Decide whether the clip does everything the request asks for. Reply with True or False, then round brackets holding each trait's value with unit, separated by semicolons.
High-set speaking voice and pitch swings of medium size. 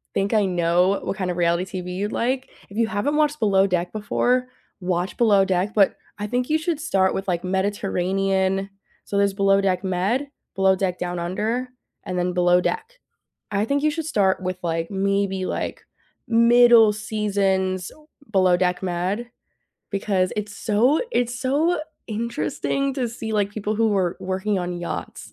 True (200 Hz; 3.7 semitones)